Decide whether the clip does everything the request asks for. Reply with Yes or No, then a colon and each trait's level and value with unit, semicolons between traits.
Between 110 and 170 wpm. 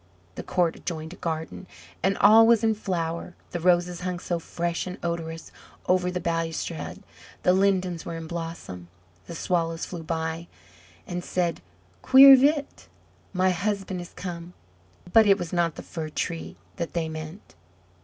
Yes: average, 155 wpm